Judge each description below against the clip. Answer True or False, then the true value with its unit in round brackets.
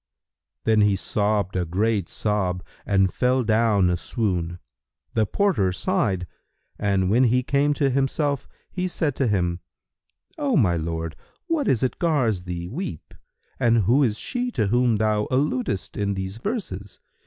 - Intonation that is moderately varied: False (5.7 semitones)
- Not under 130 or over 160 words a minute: True (155 wpm)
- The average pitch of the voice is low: True (110 Hz)